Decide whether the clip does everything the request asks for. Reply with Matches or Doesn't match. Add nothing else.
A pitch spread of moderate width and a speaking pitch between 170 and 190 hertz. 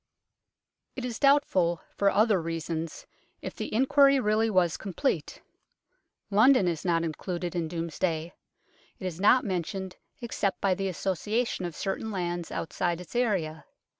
Matches